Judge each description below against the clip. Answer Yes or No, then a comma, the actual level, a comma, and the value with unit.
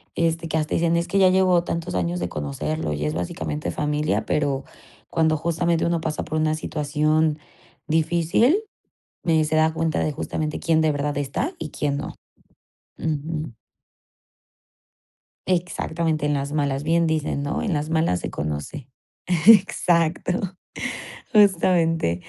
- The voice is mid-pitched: Yes, medium, 155 Hz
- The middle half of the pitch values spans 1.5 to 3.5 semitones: Yes, average, 2.7 semitones